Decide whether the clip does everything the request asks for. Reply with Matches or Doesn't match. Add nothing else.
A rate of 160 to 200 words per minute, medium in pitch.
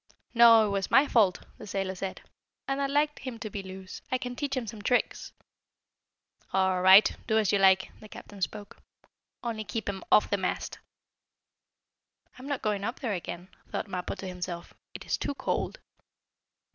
Doesn't match